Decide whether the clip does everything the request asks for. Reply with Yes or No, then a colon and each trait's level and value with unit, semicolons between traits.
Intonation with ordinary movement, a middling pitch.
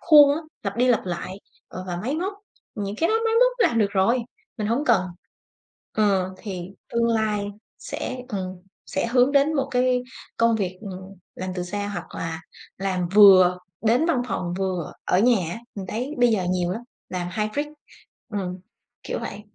No: average, 5.0 semitones; high, 210 Hz